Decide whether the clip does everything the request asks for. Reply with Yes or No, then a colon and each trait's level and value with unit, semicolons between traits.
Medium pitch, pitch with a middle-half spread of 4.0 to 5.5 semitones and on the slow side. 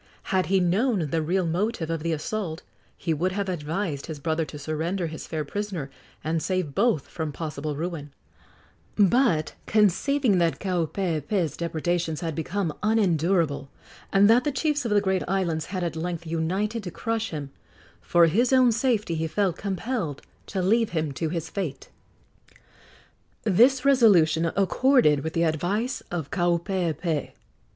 No: medium, 175 Hz; average, 4.4 semitones; average, 150 wpm